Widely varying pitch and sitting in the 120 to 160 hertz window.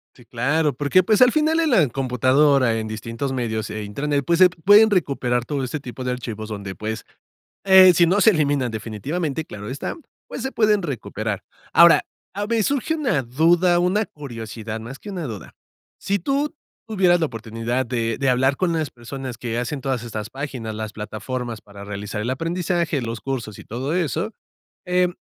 Yes: wide, 7.4 semitones; low, 135 Hz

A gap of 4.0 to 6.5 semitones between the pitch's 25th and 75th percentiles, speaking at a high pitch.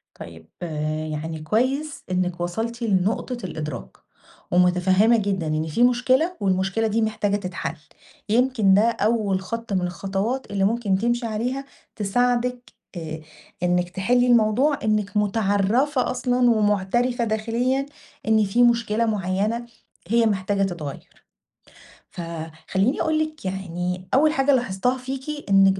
Yes: average, 4.6 semitones; high, 215 Hz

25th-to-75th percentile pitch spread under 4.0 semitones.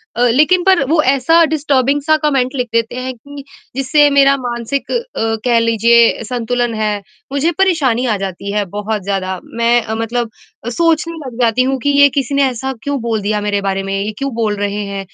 No: average, 4.3 semitones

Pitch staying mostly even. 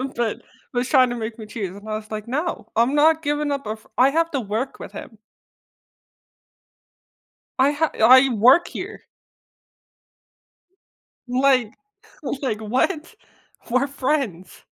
No: average, 4.4 semitones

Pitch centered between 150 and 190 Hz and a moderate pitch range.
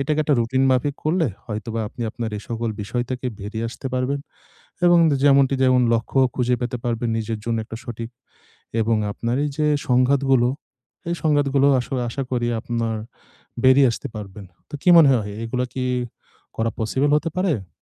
No: low, 125 Hz; average, 3.2 semitones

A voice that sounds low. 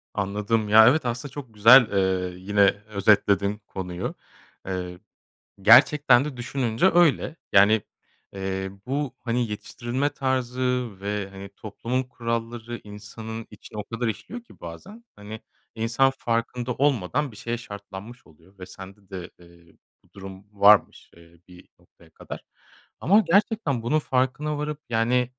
Yes: low, 115 Hz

